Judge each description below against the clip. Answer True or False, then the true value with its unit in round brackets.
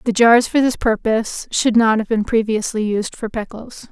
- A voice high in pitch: True (225 Hz)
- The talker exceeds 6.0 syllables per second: False (4.8 syllables/s)